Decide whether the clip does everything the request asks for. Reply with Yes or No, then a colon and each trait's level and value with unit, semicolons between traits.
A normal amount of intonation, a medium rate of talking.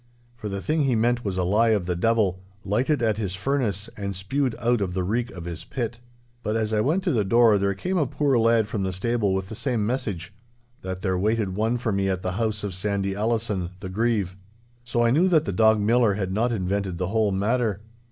No: average, 3.6 semitones; fast, 230 wpm